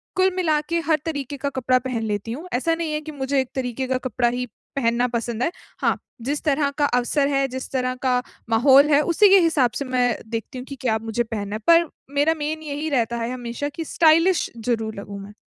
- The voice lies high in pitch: Yes, very high, 265 Hz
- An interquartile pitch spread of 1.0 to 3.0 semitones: No, average, 4.1 semitones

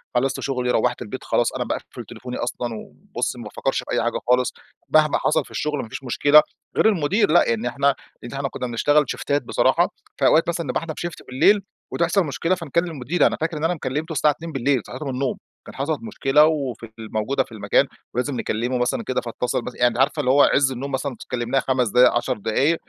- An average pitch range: Yes, average, 3.8 semitones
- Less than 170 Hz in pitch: Yes, low, 135 Hz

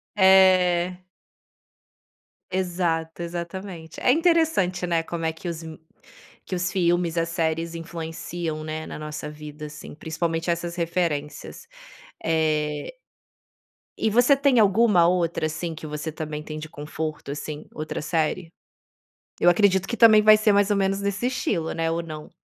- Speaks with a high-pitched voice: No, medium, 170 Hz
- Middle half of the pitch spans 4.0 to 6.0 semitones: No, average, 3.0 semitones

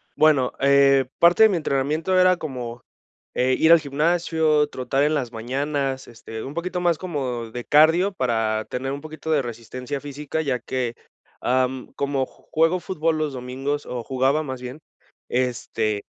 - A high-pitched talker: No, medium, 140 Hz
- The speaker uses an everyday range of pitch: Yes, average, 3.7 semitones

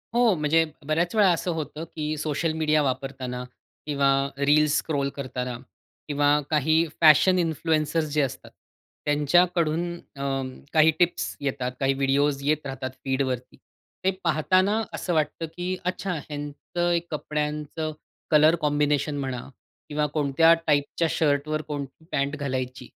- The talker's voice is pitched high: No, medium, 150 Hz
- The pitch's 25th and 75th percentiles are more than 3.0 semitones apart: No, narrow, 2.5 semitones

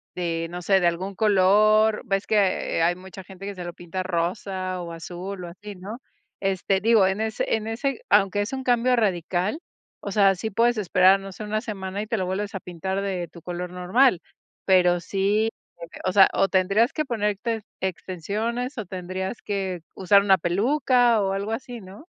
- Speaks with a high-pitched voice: Yes, high, 195 Hz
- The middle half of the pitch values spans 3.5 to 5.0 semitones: No, average, 2.8 semitones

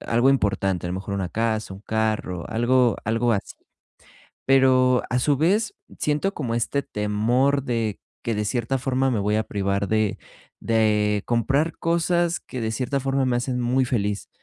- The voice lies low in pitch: Yes, low, 120 Hz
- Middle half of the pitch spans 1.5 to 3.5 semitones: No, average, 4.0 semitones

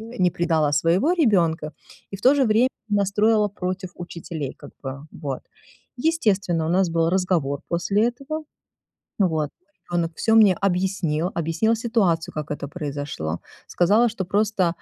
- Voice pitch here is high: No, medium, 180 Hz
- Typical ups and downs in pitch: Yes, average, 4.8 semitones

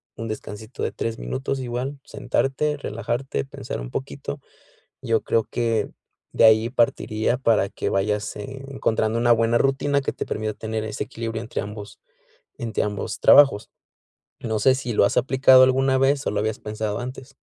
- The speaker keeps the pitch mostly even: No, average, 3.6 semitones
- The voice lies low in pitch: Yes, low, 115 Hz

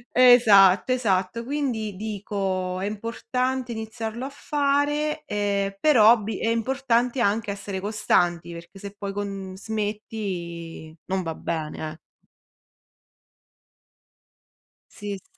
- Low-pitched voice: No, high, 210 Hz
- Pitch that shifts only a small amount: No, average, 3.8 semitones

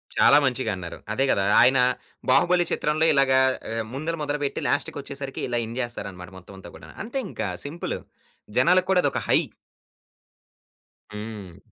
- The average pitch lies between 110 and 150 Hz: Yes, low, 135 Hz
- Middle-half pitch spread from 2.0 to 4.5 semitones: No, average, 5.1 semitones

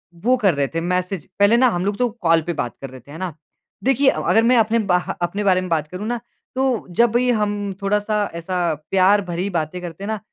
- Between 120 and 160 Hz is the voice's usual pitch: No, high, 195 Hz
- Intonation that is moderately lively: Yes, average, 4.2 semitones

